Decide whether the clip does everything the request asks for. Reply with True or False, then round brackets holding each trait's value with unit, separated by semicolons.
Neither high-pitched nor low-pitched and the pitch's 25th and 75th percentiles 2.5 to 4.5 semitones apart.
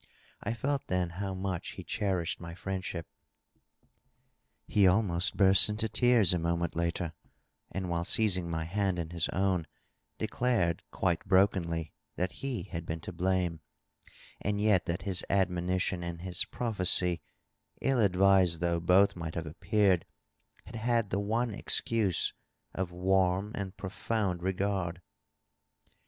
False (95 Hz; 2.9 semitones)